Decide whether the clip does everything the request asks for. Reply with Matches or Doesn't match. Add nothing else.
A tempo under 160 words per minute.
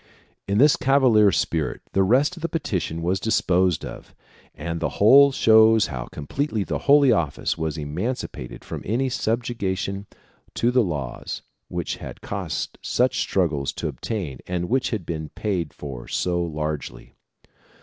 Matches